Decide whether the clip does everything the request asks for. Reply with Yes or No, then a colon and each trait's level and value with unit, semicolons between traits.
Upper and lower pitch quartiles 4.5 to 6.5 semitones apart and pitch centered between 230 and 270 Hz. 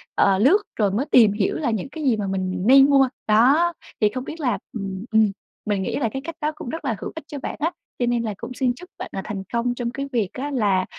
Yes: average, 4.9 semitones; high, 240 Hz